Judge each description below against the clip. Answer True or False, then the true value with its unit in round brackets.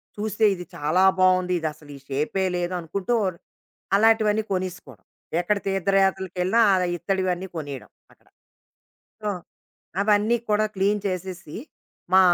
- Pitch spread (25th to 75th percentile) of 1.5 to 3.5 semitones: True (2.8 semitones)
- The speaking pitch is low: False (185 Hz)